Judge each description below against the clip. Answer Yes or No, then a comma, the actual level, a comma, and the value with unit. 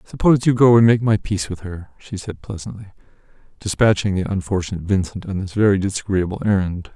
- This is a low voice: Yes, low, 100 Hz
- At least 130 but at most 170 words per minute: No, average, 180 wpm